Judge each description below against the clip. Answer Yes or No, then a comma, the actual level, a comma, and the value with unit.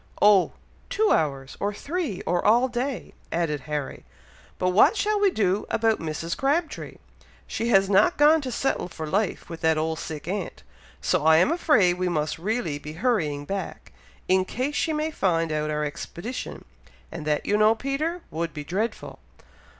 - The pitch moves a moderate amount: No, wide, 8.0 semitones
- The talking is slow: No, average, 175 wpm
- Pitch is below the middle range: No, high, 190 Hz